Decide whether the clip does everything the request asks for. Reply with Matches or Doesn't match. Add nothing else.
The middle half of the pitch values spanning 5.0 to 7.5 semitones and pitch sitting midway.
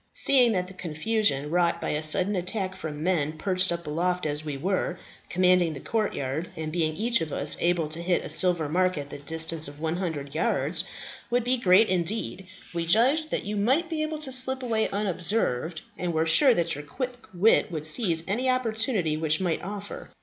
Matches